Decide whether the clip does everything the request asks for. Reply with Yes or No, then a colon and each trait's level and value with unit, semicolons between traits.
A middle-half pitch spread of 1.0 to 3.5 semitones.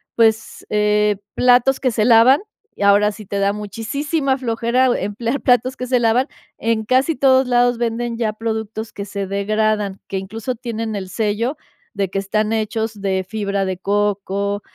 Yes: average, 3.0 semitones